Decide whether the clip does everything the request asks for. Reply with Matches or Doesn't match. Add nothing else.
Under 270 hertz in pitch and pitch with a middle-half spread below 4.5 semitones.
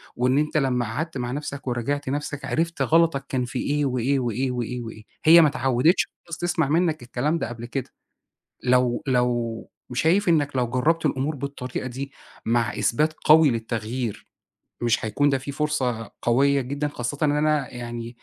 Matches